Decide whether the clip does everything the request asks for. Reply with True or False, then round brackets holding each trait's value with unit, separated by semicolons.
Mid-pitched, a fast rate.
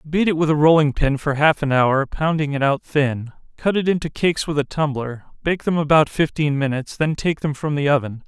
True (150 Hz; 220 wpm)